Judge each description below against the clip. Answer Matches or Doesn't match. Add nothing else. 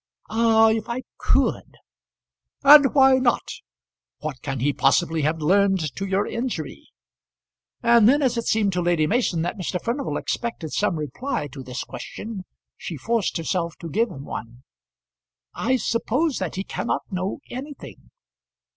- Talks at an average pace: Matches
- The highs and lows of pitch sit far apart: Matches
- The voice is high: Matches